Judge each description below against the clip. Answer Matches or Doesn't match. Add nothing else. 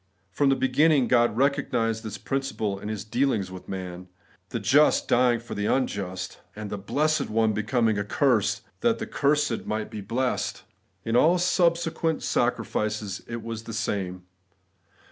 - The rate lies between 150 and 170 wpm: Matches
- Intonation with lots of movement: Doesn't match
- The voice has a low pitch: Matches